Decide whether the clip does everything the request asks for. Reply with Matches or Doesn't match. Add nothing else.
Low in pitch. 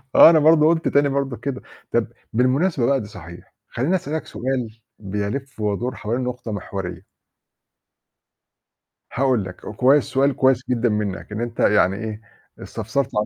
Matches